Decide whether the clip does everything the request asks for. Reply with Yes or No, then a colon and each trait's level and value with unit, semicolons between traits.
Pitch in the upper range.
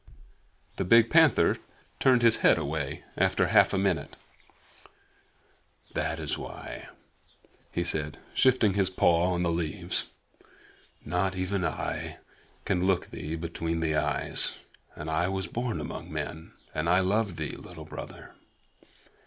No: very low, 90 Hz